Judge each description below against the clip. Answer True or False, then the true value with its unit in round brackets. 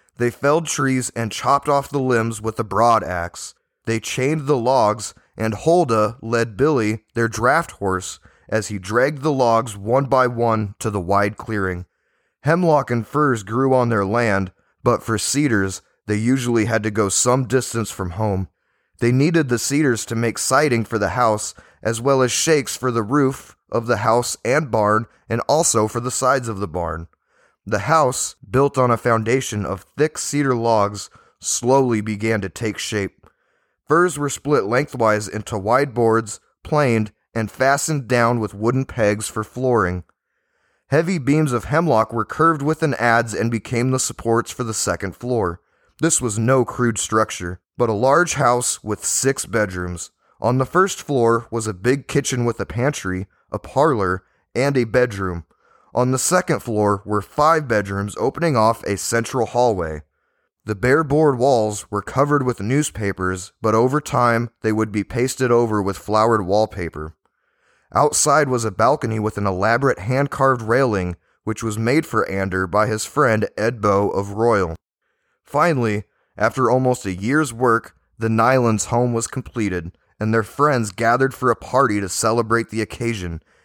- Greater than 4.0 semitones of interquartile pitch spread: False (3.6 semitones)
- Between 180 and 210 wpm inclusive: False (165 wpm)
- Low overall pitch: True (115 Hz)